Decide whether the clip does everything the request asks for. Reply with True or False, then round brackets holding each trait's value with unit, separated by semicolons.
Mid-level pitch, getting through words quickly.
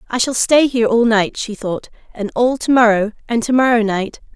False (230 Hz; 220 wpm)